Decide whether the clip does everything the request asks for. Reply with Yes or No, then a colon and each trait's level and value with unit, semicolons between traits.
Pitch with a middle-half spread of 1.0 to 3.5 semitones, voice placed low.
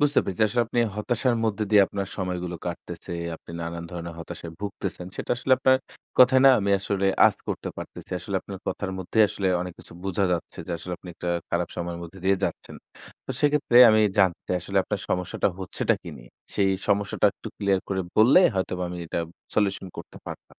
Yes: average, 3.2 semitones; very low, 95 Hz